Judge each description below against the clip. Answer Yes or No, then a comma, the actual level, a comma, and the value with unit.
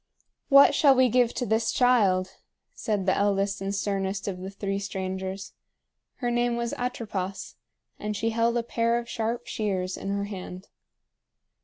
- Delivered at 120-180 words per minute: Yes, average, 160 wpm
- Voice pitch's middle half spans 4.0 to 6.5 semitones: No, average, 3.4 semitones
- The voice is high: Yes, high, 205 Hz